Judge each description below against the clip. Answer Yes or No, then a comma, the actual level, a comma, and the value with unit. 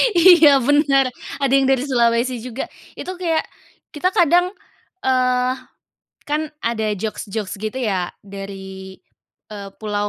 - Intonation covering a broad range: Yes, wide, 5.7 semitones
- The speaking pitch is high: Yes, very high, 250 Hz